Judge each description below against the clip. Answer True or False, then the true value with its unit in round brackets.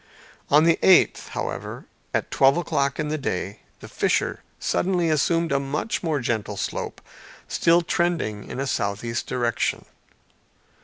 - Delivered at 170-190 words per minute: False (140 wpm)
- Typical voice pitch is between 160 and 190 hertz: False (140 Hz)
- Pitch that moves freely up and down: True (5.9 semitones)